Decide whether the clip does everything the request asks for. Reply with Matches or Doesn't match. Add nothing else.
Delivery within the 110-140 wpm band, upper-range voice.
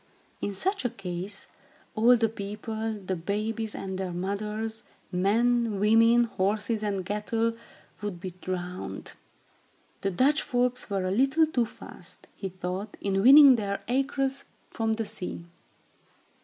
Matches